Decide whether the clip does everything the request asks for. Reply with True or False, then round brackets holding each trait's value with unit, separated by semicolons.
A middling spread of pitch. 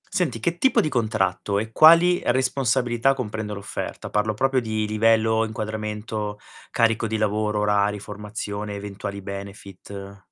False (2.1 semitones)